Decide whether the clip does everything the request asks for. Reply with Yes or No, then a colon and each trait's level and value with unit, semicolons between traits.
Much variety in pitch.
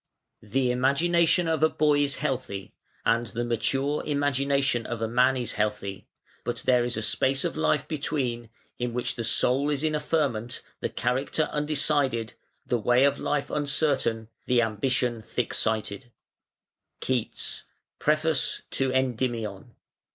No: average, 3.6 semitones